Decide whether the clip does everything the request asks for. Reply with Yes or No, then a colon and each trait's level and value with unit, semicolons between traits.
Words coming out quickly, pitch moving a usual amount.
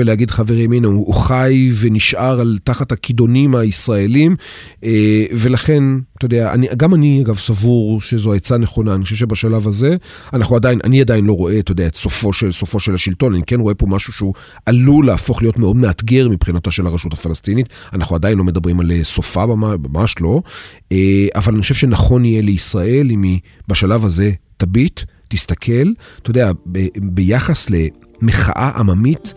Yes: fast, 160 wpm; average, 4.2 semitones